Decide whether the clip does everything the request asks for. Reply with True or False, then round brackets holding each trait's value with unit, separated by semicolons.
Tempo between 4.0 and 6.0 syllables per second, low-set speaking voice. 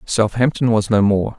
True (4.7 syllables/s; 110 Hz)